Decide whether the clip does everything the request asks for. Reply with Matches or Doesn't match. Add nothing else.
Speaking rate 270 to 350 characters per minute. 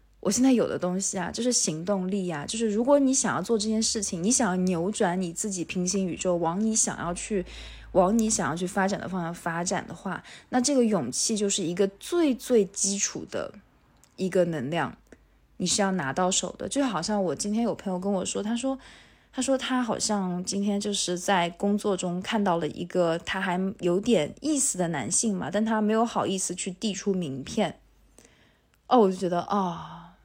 Matches